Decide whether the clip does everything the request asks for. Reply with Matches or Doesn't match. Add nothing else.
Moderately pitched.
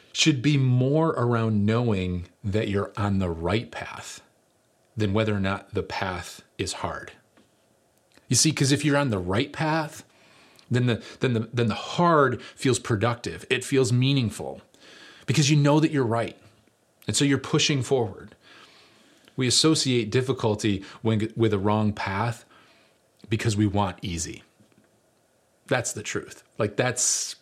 Doesn't match